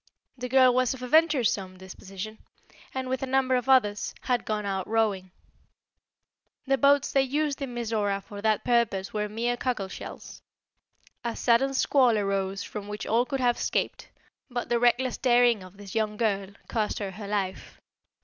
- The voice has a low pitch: No, high, 230 Hz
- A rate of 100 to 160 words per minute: No, average, 170 wpm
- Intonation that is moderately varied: Yes, average, 3.9 semitones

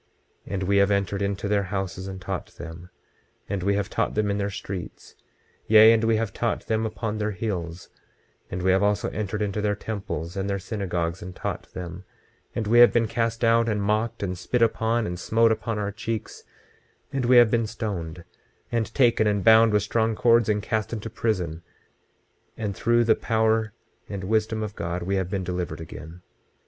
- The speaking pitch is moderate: No, low, 105 Hz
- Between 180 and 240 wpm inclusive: Yes, average, 195 wpm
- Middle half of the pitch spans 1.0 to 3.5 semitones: Yes, average, 3.0 semitones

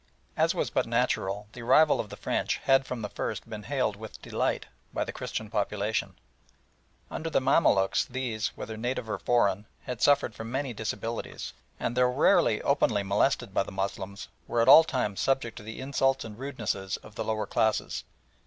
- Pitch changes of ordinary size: Yes, average, 3.9 semitones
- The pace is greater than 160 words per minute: Yes, average, 180 wpm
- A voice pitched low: Yes, low, 110 Hz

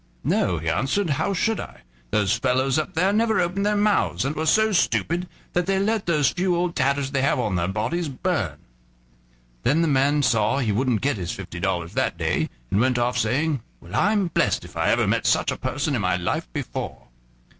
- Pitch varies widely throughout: Yes, wide, 7.9 semitones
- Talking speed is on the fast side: Yes, fast, 210 wpm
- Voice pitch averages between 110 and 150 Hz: Yes, medium, 140 Hz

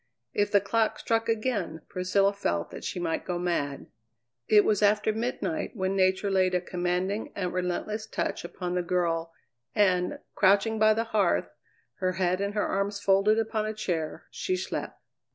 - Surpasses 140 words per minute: Yes, average, 170 wpm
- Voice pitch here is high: Yes, high, 195 Hz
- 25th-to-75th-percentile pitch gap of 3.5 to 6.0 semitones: No, average, 3.0 semitones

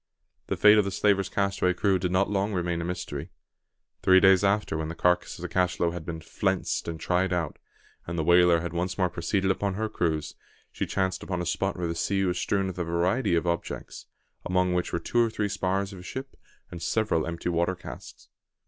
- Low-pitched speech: Yes, very low, 90 Hz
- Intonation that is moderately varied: No, narrow, 2.2 semitones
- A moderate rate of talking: No, fast, 220 wpm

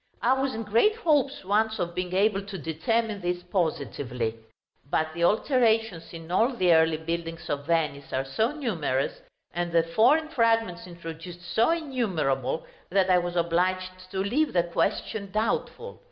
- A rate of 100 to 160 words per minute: Yes, average, 155 wpm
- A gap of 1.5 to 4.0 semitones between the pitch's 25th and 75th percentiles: No, average, 5.2 semitones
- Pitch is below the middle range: No, medium, 185 Hz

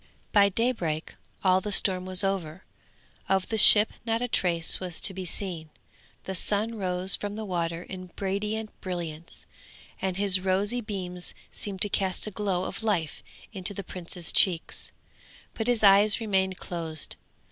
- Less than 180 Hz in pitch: No, high, 190 Hz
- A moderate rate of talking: Yes, average, 160 wpm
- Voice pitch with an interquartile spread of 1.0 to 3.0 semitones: Yes, narrow, 2.4 semitones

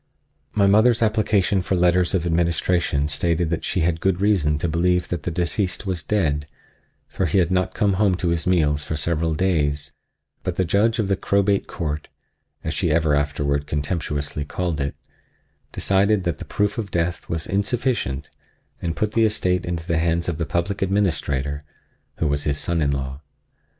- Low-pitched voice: Yes, very low, 85 Hz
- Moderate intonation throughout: Yes, average, 4.1 semitones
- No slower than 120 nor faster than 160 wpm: No, average, 175 wpm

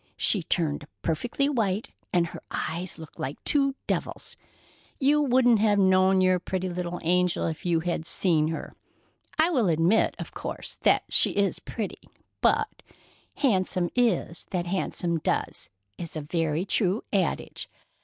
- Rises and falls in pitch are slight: No, average, 4.3 semitones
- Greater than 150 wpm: No, average, 145 wpm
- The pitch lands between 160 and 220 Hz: Yes, medium, 185 Hz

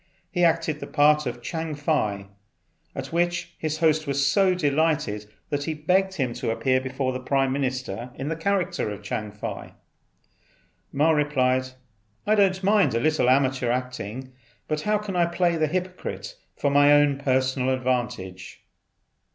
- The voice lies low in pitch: No, medium, 145 Hz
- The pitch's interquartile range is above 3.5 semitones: Yes, average, 4.2 semitones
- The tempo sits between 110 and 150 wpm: No, average, 160 wpm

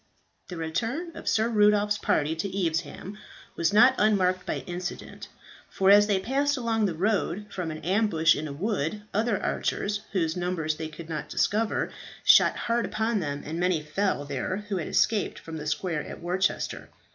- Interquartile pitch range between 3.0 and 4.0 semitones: No, average, 4.6 semitones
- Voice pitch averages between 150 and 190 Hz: Yes, medium, 185 Hz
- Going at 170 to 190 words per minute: Yes, average, 175 wpm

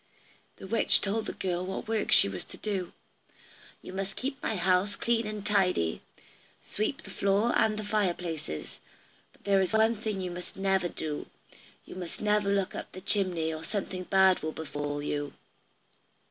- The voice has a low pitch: No, high, 190 Hz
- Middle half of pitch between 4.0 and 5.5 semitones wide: No, average, 3.2 semitones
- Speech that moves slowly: No, average, 175 wpm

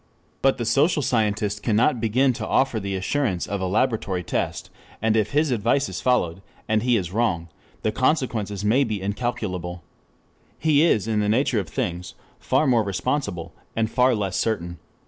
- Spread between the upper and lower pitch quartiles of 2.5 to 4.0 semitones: No, average, 4.5 semitones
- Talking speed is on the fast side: No, average, 170 wpm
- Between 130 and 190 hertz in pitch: No, low, 110 Hz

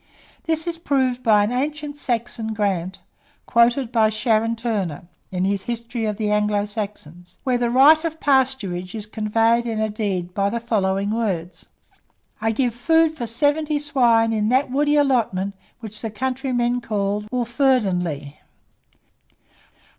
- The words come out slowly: No, average, 145 wpm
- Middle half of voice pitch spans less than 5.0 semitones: Yes, average, 3.9 semitones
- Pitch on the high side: Yes, high, 230 Hz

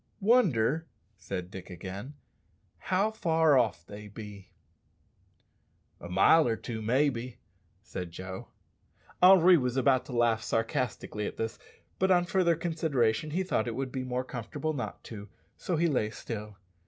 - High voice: No, low, 125 Hz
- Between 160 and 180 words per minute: No, average, 145 wpm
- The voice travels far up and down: Yes, wide, 7.0 semitones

